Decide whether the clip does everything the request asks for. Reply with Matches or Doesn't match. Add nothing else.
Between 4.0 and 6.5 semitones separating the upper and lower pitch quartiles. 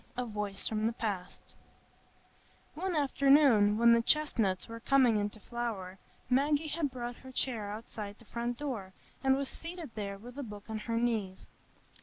Matches